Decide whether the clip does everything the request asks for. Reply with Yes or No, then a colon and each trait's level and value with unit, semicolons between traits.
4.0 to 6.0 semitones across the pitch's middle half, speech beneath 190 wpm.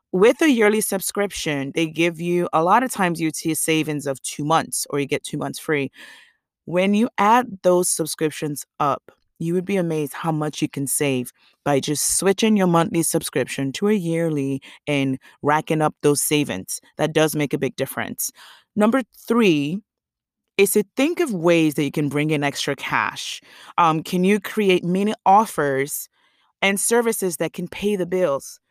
Yes: average, 5.0 semitones; average, 180 wpm